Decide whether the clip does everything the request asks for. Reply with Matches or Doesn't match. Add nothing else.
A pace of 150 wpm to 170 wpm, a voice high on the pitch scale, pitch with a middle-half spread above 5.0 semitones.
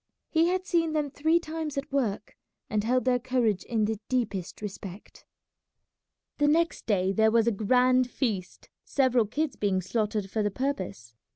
Matches